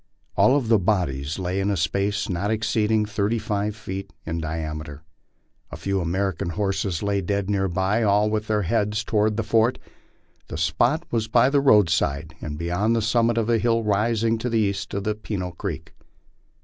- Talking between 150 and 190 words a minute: Yes, average, 175 wpm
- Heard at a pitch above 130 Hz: No, low, 105 Hz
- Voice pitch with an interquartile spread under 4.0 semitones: Yes, average, 3.5 semitones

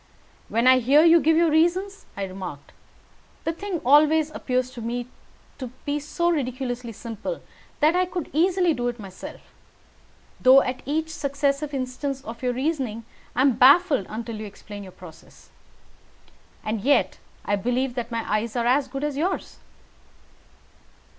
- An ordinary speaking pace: Yes, average, 150 wpm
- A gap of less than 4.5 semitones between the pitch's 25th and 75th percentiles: No, average, 5.0 semitones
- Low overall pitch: No, very high, 260 Hz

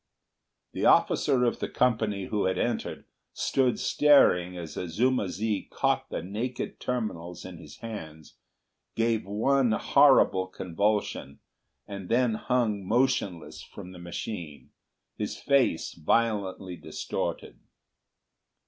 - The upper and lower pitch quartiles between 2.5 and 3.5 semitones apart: No, average, 4.9 semitones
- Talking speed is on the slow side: Yes, slow, 110 wpm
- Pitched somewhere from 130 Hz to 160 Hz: No, low, 105 Hz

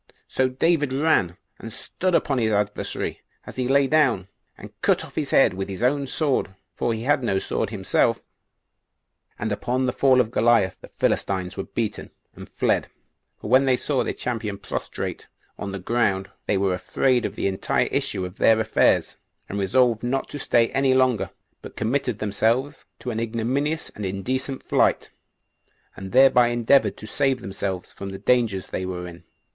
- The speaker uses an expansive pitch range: No, average, 4.9 semitones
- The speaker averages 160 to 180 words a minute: Yes, average, 175 wpm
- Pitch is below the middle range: Yes, low, 115 Hz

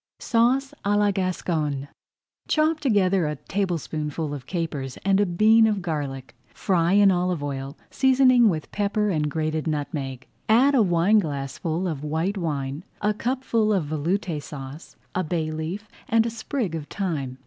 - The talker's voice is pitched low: No, medium, 175 Hz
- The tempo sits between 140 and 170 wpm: Yes, average, 150 wpm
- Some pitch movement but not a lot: No, wide, 5.7 semitones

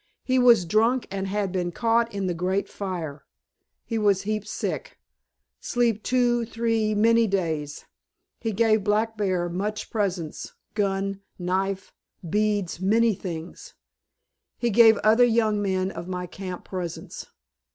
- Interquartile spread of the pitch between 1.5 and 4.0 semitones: Yes, average, 3.4 semitones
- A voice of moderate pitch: No, high, 205 Hz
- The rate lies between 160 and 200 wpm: No, slow, 135 wpm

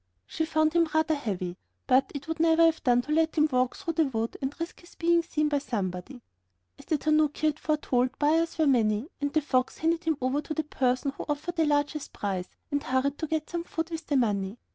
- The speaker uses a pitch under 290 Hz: No, very high, 295 Hz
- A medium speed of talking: No, fast, 230 wpm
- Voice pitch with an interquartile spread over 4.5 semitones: No, average, 4.0 semitones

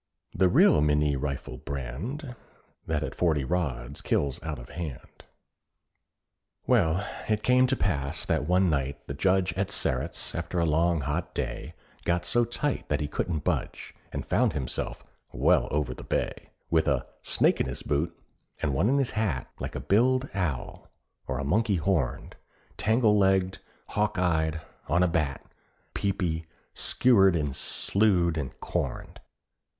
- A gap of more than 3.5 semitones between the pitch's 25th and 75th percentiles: Yes, average, 5.0 semitones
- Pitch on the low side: Yes, very low, 85 Hz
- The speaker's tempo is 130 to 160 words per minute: Yes, average, 155 wpm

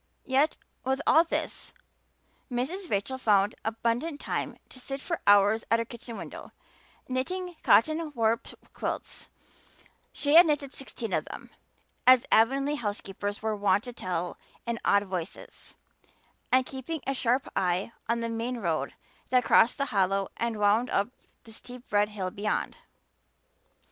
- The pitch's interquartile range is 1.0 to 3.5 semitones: No, average, 4.5 semitones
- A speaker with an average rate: Yes, average, 145 wpm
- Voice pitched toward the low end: No, high, 235 Hz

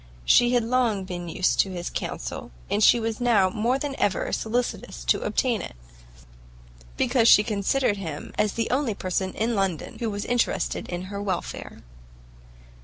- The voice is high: Yes, high, 210 Hz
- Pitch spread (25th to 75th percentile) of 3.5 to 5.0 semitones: Yes, average, 4.2 semitones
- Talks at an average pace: Yes, average, 165 wpm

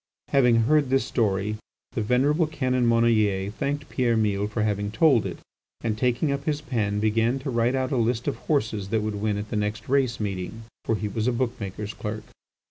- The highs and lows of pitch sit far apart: No, average, 3.4 semitones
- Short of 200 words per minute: No, fast, 205 wpm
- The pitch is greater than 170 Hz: No, low, 115 Hz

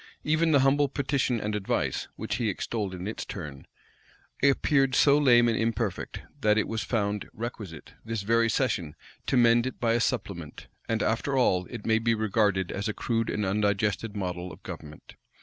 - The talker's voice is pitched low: Yes, low, 110 Hz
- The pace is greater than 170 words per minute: Yes, average, 180 wpm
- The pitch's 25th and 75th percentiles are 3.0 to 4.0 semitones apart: Yes, average, 3.4 semitones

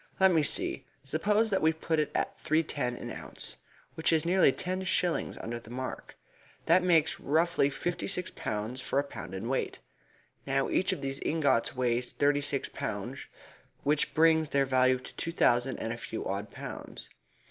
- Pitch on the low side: No, medium, 145 Hz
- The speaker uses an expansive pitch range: No, average, 4.5 semitones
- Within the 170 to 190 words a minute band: Yes, average, 180 wpm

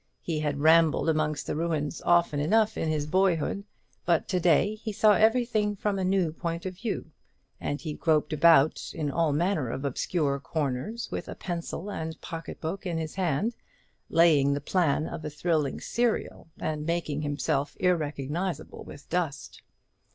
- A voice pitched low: No, medium, 165 Hz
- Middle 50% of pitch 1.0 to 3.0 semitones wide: No, average, 3.6 semitones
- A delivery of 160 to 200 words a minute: Yes, average, 165 wpm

